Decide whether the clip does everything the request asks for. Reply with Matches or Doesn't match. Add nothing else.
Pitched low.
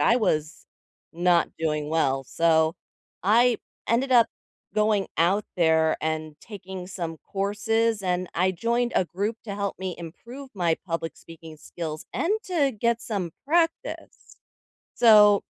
Doesn't match